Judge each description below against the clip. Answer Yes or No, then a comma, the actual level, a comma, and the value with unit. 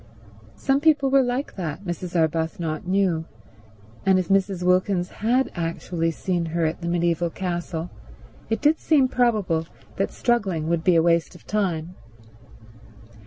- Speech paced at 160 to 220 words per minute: No, average, 145 wpm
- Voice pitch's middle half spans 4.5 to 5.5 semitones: No, average, 3.9 semitones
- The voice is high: No, medium, 180 Hz